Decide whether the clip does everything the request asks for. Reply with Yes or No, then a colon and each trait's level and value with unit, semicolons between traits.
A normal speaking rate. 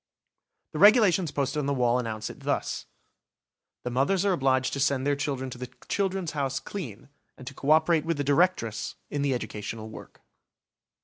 Yes: average, 185 wpm